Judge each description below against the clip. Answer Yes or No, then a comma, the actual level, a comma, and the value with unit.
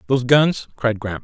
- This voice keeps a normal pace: Yes, average, 195 wpm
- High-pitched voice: No, low, 125 Hz